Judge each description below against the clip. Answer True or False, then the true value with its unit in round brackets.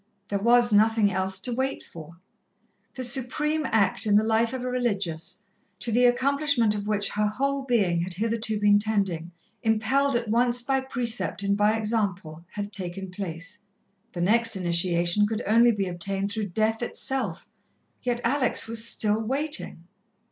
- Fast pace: False (160 wpm)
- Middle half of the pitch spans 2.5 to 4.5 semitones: True (3.7 semitones)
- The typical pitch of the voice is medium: False (215 Hz)